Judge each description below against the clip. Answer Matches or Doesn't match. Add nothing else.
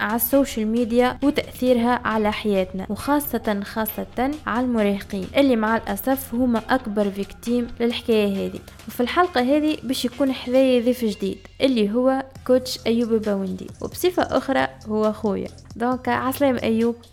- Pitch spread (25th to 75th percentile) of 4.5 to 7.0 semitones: Doesn't match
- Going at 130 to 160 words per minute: Matches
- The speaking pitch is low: Doesn't match